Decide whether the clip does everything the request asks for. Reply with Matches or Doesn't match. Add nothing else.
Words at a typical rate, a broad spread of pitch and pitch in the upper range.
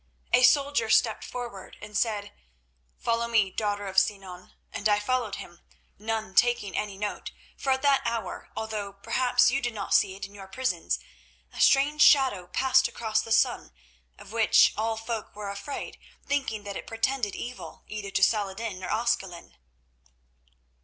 Doesn't match